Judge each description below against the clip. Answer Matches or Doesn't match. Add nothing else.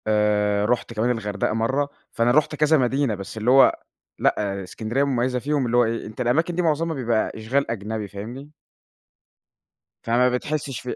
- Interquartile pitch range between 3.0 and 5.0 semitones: Matches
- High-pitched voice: Doesn't match